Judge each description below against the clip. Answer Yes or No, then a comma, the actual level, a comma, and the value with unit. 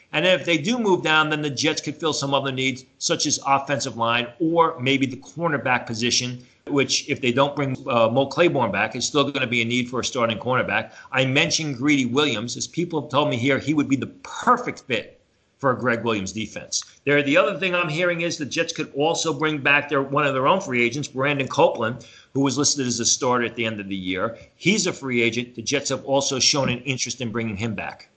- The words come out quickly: Yes, fast, 240 wpm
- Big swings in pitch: No, average, 3.5 semitones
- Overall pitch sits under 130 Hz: No, low, 135 Hz